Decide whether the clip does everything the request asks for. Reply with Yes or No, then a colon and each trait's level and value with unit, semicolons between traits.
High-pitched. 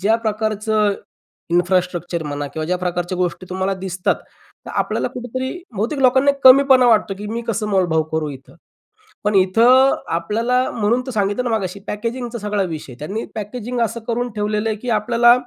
Yes: high, 210 Hz